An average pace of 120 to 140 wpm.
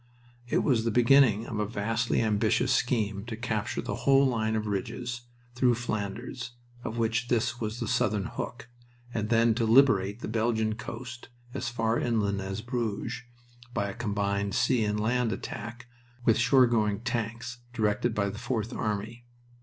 No: average, 160 wpm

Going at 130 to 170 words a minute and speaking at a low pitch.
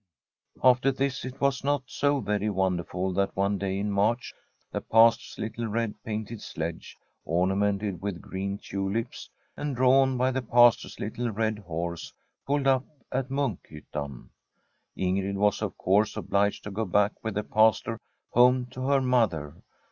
Yes: average, 150 wpm; low, 105 Hz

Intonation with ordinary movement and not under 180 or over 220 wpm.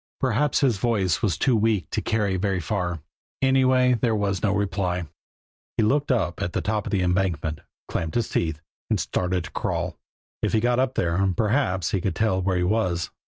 Yes: average, 4.1 semitones; average, 195 wpm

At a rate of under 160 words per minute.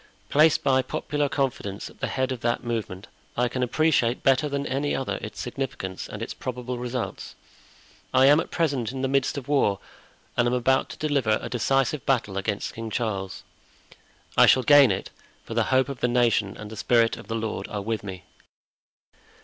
No: average, 190 wpm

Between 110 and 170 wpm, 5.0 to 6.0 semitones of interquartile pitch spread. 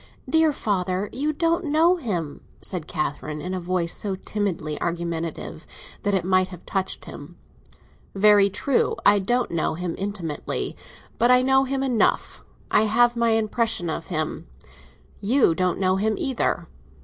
Yes: average, 150 wpm; wide, 5.6 semitones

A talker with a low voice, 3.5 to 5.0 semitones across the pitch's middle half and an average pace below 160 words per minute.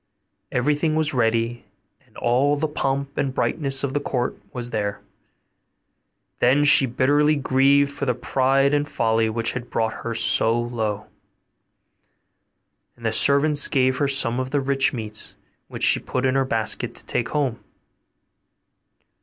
No: low, 130 Hz; average, 3.1 semitones; average, 150 wpm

